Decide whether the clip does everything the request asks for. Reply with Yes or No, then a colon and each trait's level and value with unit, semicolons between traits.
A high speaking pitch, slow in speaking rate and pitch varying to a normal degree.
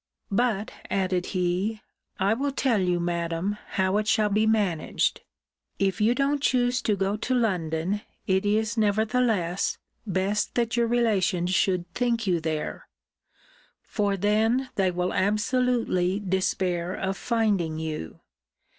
Yes: high, 200 Hz; slow, 130 wpm; average, 3.7 semitones